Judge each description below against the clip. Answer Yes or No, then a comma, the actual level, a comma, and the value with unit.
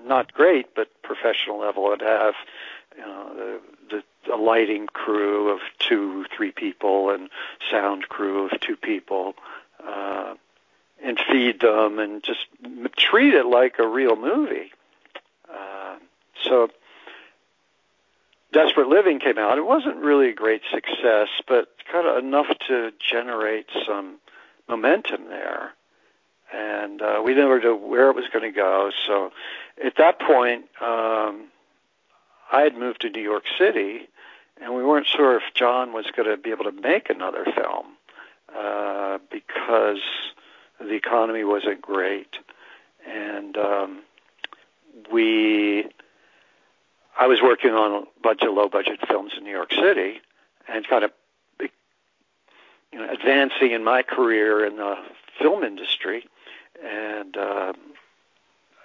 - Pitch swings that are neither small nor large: Yes, average, 3.5 semitones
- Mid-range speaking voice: No, low, 110 Hz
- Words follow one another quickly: No, slow, 135 wpm